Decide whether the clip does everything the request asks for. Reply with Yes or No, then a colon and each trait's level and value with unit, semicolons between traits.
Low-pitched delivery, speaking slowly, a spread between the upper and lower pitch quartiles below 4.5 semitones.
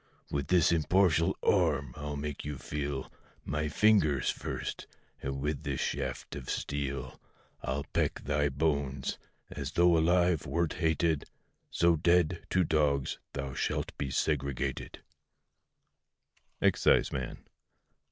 Yes: very low, 75 Hz; slow, 115 wpm; average, 2.9 semitones